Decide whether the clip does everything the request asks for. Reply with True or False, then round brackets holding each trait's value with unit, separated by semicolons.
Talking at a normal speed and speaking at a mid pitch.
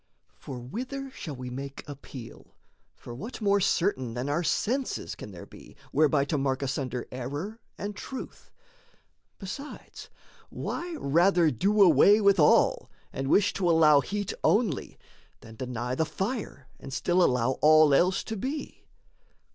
True (145 wpm; 155 Hz)